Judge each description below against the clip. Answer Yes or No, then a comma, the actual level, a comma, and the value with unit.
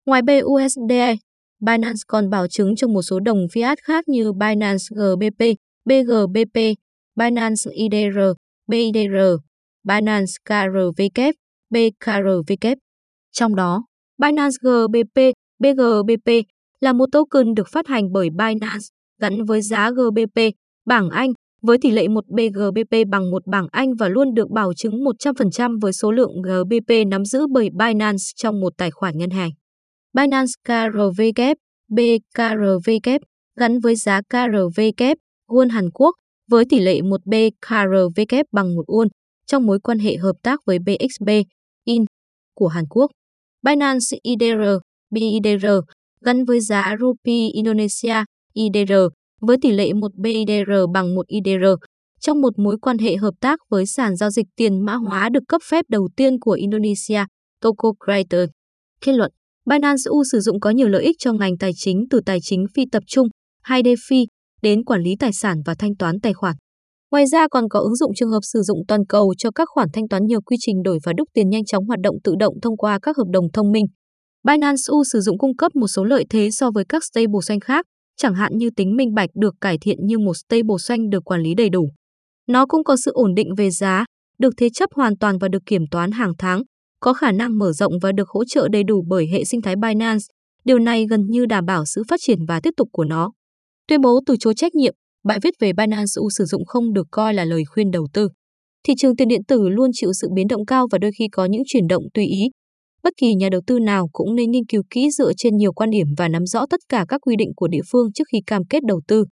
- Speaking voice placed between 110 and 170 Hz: No, high, 220 Hz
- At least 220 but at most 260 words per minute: No, average, 200 wpm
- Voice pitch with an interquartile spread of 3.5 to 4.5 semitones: Yes, average, 3.8 semitones